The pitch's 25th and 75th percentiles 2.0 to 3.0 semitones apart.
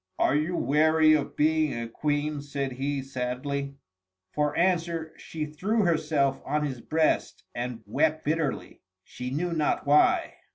Yes: narrow, 2.4 semitones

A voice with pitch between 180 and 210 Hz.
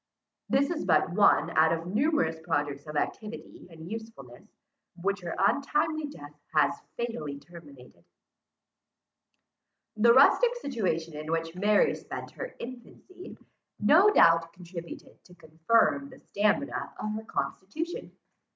Yes: high, 190 Hz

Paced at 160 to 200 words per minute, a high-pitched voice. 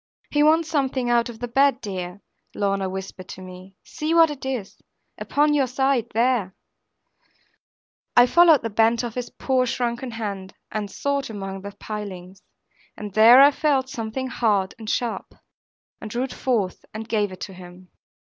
Yes: average, 165 wpm; high, 230 Hz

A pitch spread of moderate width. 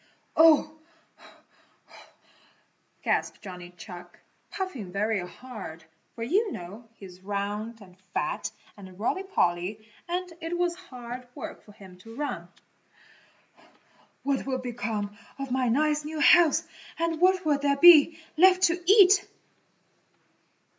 No: wide, 8.4 semitones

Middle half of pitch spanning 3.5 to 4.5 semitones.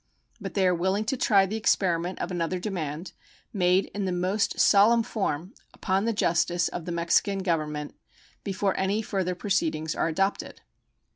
No: average, 2.8 semitones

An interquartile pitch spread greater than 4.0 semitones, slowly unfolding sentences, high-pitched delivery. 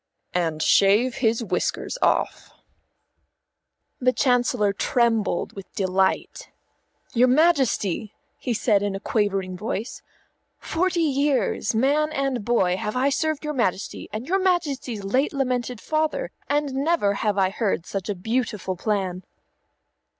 Yes: wide, 5.6 semitones; slow, 130 wpm; high, 235 Hz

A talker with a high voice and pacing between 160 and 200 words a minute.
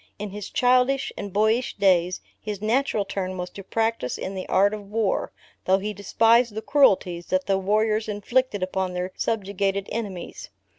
Yes: high, 205 Hz; average, 165 wpm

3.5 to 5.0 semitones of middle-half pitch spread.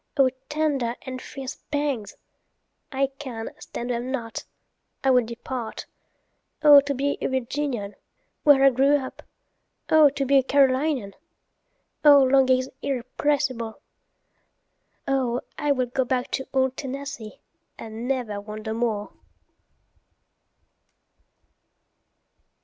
No: average, 2.8 semitones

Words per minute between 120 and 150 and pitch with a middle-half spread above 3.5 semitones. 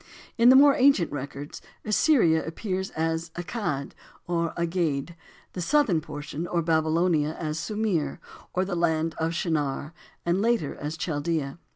No: average, 140 wpm; average, 3.2 semitones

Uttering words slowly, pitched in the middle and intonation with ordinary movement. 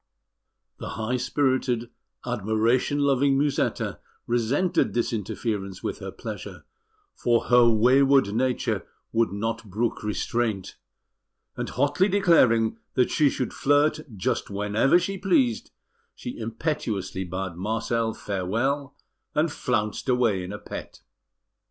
No: slow, 115 wpm; low, 120 Hz; average, 4.3 semitones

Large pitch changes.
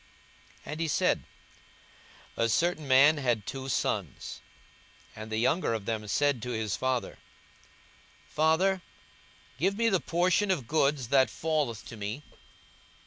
Yes: wide, 5.7 semitones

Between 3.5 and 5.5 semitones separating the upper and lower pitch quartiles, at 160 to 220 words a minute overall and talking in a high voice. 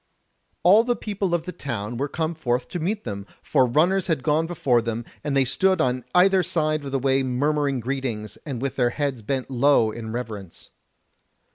No: average, 5.0 semitones; average, 190 wpm; low, 135 Hz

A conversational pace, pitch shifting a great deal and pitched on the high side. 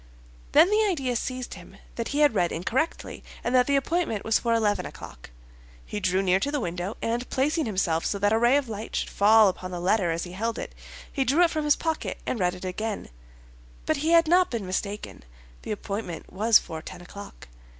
No: fast, 215 wpm; wide, 6.8 semitones; high, 225 Hz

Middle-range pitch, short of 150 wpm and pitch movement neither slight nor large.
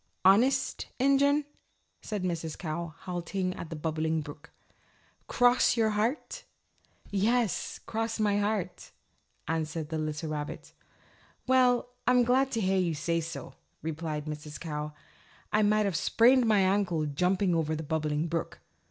No: medium, 180 Hz; slow, 135 wpm; wide, 5.9 semitones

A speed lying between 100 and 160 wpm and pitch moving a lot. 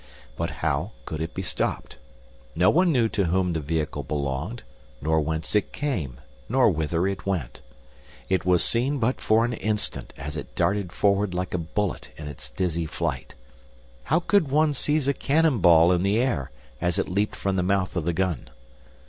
No: average, 185 wpm; wide, 5.8 semitones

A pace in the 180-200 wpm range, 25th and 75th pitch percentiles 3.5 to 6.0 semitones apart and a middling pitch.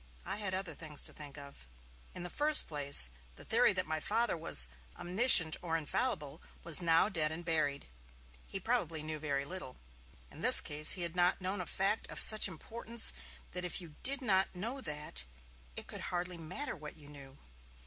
Yes: average, 190 wpm; average, 4.3 semitones; medium, 170 Hz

